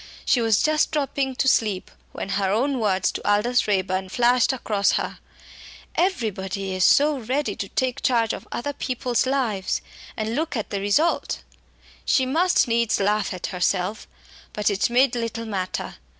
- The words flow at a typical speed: Yes, average, 160 wpm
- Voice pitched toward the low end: No, high, 230 Hz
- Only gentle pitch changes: No, average, 4.8 semitones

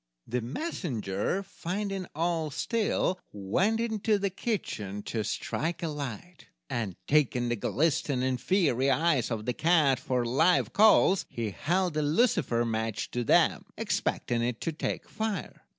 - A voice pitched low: No, medium, 150 Hz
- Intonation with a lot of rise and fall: Yes, wide, 7.6 semitones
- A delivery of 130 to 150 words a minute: Yes, average, 140 wpm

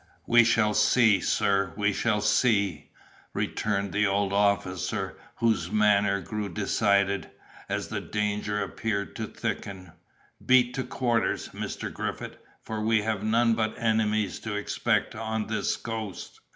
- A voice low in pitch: Yes, low, 105 Hz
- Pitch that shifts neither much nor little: No, narrow, 1.9 semitones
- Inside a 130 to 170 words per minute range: Yes, slow, 135 wpm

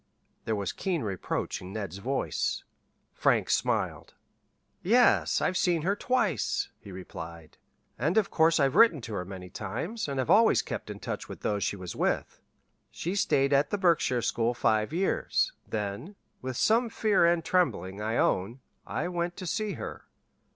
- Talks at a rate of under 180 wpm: Yes, average, 165 wpm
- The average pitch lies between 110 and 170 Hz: Yes, medium, 140 Hz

